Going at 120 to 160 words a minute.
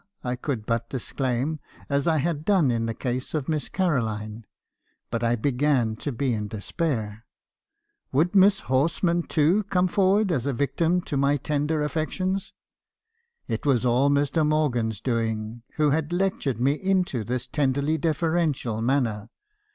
Yes: average, 150 wpm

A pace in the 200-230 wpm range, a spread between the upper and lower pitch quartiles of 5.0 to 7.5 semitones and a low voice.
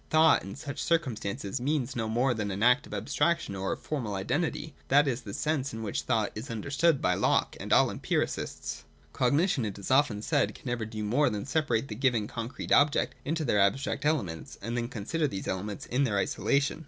Yes: fast, 205 wpm; wide, 5.4 semitones; low, 125 Hz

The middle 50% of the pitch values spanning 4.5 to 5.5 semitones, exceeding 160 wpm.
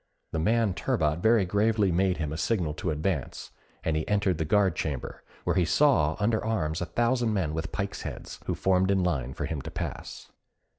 Yes: average, 5.1 semitones; average, 200 wpm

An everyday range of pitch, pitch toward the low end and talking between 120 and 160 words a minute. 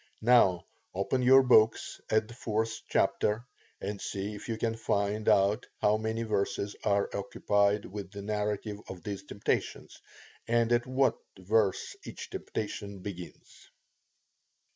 No: narrow, 2.0 semitones; low, 105 Hz; slow, 135 wpm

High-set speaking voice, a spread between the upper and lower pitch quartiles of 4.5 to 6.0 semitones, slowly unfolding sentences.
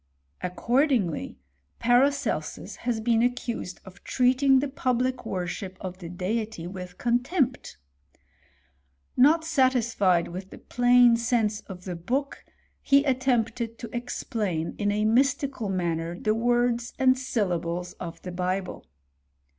Yes: high, 230 Hz; wide, 5.4 semitones; slow, 125 wpm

